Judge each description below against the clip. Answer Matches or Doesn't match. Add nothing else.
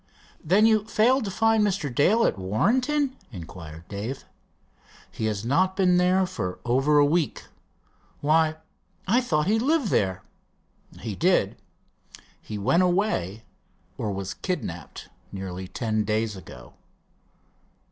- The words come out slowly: Matches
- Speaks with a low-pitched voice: Doesn't match